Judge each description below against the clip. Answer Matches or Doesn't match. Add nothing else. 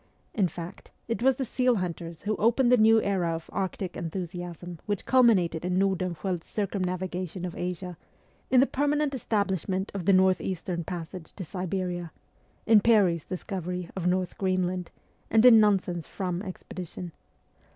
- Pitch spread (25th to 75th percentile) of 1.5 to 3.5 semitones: Matches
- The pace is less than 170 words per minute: Matches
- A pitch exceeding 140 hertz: Matches